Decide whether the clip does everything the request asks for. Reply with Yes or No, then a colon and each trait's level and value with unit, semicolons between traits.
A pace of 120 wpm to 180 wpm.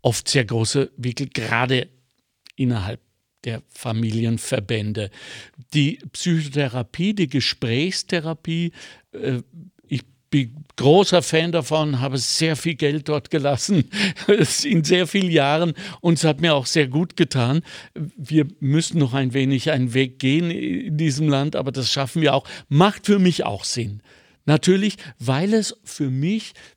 Yes: average, 135 wpm